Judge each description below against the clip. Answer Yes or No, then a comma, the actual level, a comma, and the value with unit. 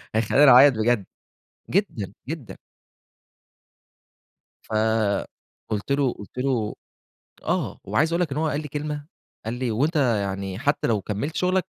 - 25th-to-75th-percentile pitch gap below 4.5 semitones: No, wide, 5.4 semitones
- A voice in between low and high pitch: No, low, 125 Hz